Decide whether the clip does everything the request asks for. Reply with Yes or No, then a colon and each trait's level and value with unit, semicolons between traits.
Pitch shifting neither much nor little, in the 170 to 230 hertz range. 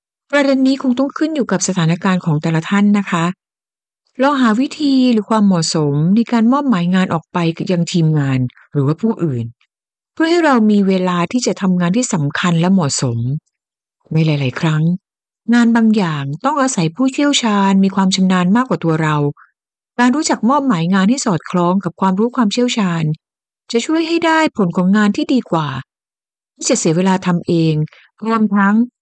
No: wide, 6.7 semitones; high, 190 Hz